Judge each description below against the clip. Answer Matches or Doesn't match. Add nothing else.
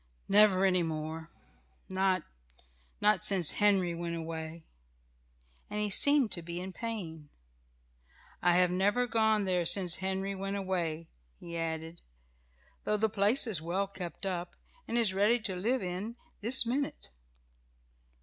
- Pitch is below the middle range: Doesn't match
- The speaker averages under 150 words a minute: Matches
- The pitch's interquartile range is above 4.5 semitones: Doesn't match